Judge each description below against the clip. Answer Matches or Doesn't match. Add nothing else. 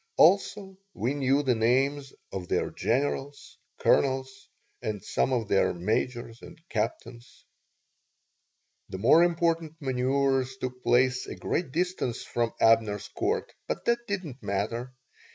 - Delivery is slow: Matches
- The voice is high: Doesn't match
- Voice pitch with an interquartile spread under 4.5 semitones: Matches